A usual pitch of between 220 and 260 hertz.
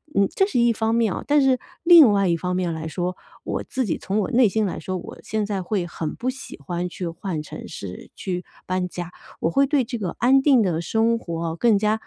No: high, 200 Hz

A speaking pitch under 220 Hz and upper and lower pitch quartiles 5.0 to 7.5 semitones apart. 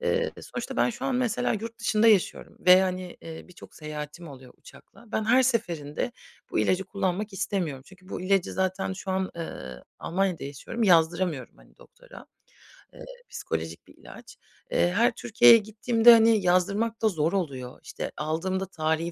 Yes: high, 190 Hz; wide, 5.4 semitones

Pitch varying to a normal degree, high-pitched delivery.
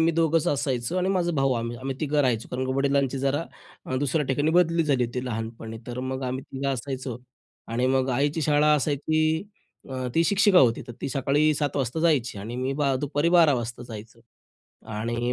No: average, 3.6 semitones; low, 135 Hz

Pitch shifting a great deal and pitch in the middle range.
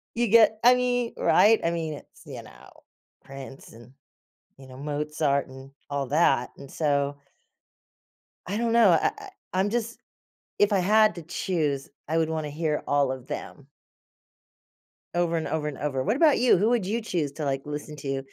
Yes: wide, 6.9 semitones; medium, 155 Hz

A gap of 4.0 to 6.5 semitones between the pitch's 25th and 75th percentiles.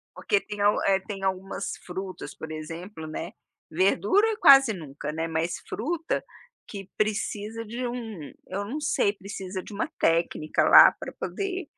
Yes: average, 4.8 semitones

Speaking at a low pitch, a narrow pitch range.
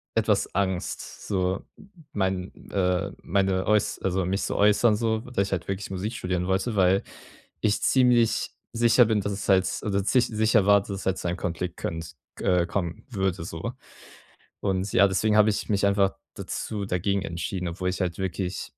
Yes: very low, 95 Hz; narrow, 2.2 semitones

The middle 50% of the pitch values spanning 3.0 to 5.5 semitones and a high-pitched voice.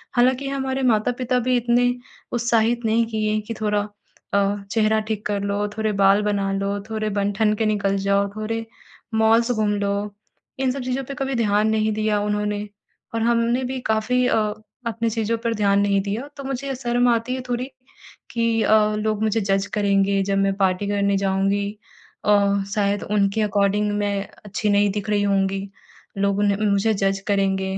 No: narrow, 2.4 semitones; high, 210 Hz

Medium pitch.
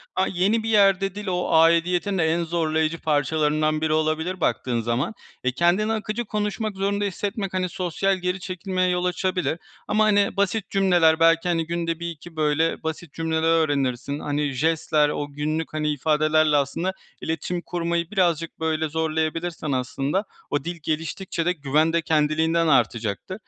Yes: medium, 165 Hz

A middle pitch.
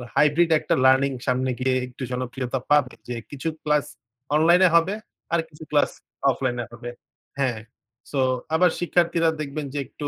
Yes: medium, 145 Hz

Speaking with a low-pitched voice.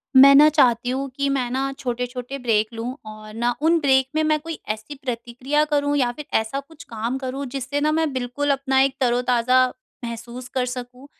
No: very high, 260 Hz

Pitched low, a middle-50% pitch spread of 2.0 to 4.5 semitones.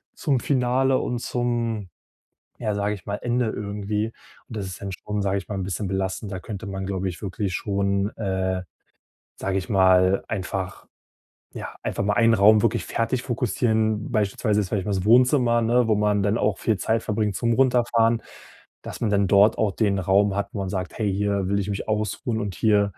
Yes: low, 105 Hz; narrow, 2.6 semitones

